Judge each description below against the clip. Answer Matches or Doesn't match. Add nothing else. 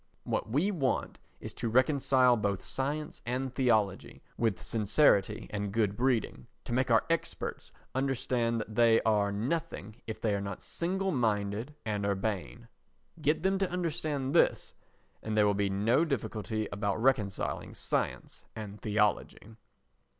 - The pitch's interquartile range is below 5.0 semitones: Matches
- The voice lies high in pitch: Doesn't match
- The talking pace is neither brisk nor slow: Matches